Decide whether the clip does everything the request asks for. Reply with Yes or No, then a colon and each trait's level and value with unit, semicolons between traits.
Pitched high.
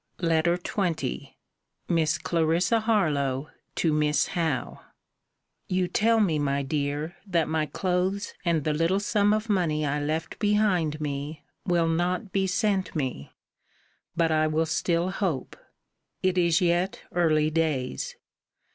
No: medium, 165 Hz